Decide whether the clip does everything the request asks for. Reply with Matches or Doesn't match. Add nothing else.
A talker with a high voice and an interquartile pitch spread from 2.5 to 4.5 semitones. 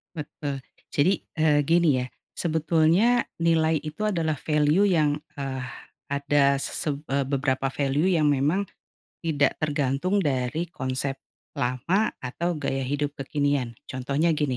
Doesn't match